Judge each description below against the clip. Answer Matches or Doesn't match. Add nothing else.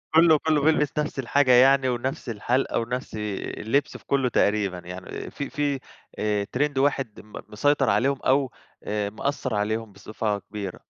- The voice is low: Matches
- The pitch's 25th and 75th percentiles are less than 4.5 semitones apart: Doesn't match